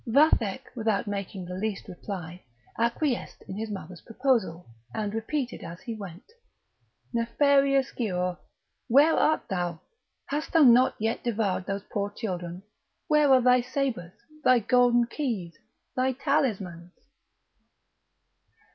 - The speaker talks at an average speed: No, slow, 120 wpm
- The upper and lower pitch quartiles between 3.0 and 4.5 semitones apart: No, wide, 5.4 semitones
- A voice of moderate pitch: No, high, 225 Hz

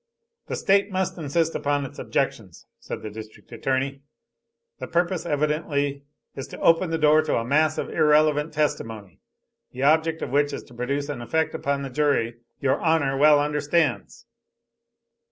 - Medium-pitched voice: Yes, medium, 145 Hz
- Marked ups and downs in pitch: No, average, 2.7 semitones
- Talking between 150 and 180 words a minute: Yes, average, 160 wpm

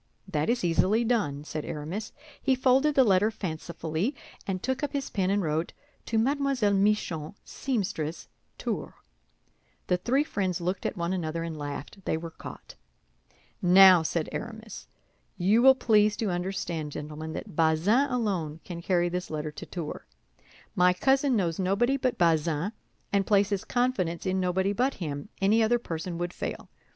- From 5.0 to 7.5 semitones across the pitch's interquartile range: Yes, average, 5.3 semitones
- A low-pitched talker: No, medium, 185 Hz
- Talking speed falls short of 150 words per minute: No, average, 160 wpm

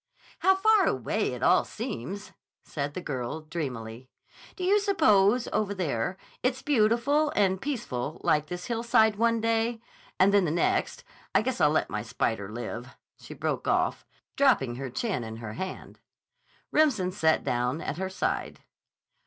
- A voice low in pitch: No, high, 190 Hz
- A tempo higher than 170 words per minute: No, average, 155 wpm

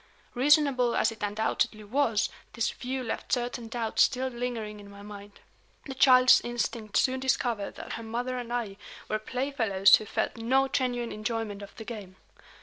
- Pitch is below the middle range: No, high, 235 Hz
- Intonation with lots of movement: No, average, 3.0 semitones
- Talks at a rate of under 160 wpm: No, average, 165 wpm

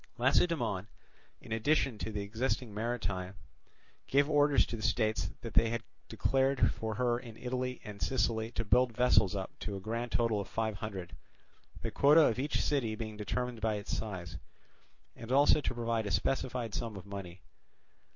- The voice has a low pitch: Yes, low, 115 Hz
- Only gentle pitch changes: No, average, 3.3 semitones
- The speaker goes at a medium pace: Yes, average, 170 wpm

